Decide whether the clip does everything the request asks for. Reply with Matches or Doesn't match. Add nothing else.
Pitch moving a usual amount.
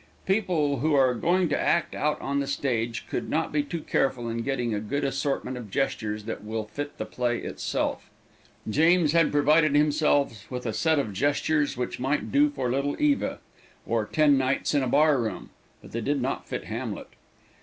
Matches